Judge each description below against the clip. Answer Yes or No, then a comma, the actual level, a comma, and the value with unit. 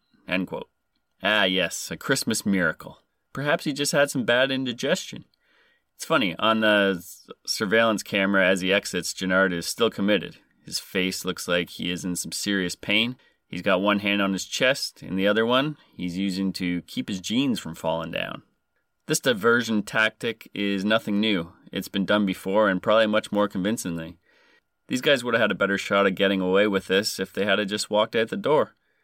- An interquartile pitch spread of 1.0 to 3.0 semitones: Yes, average, 2.7 semitones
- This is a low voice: Yes, low, 100 Hz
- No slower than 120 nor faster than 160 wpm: No, average, 190 wpm